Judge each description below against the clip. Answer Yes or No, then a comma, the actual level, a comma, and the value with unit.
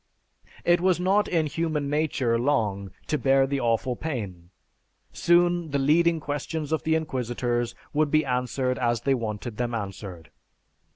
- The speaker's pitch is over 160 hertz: No, low, 135 Hz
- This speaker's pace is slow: No, average, 150 wpm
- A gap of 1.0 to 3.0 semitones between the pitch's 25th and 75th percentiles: No, average, 5.0 semitones